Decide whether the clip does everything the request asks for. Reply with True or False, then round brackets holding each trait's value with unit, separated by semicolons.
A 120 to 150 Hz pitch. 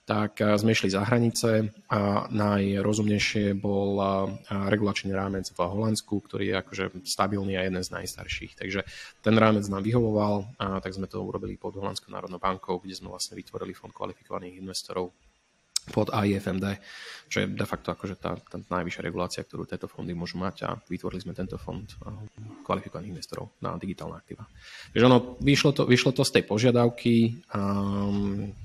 False (100 Hz)